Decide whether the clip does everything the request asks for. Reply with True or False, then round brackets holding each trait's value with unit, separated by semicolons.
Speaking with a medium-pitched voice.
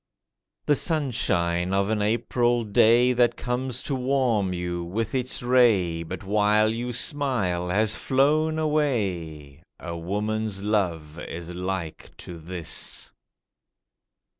False (105 Hz)